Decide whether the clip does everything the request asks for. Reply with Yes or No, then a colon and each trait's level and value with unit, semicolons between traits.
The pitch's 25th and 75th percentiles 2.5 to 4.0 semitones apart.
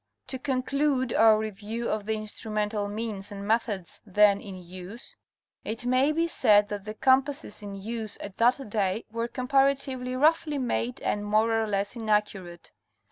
Yes: average, 3.7 semitones